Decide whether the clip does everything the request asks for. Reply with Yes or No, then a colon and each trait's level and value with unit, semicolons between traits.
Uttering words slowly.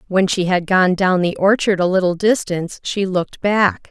No: average, 200 wpm